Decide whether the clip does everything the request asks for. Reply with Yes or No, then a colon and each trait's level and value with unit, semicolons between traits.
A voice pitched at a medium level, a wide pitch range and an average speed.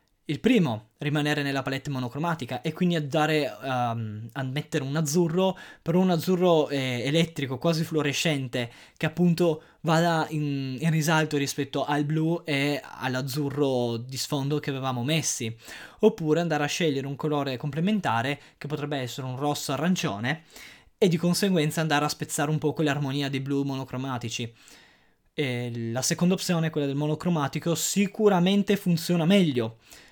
No: medium, 150 Hz; average, 3.6 semitones; average, 140 wpm